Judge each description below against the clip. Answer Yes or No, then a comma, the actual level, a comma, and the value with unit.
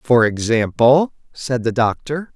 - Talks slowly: Yes, slow, 125 wpm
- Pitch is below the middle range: Yes, low, 125 Hz